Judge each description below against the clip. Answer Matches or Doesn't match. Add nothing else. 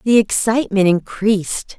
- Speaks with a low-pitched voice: Doesn't match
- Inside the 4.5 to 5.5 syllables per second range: Matches